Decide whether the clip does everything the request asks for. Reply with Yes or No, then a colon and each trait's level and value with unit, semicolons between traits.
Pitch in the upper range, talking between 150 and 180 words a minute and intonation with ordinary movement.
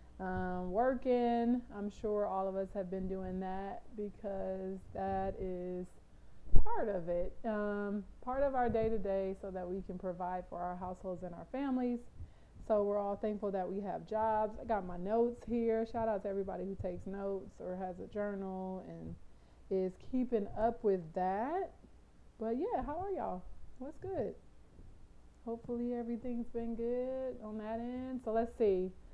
Yes: high, 205 Hz; average, 170 wpm; average, 3.7 semitones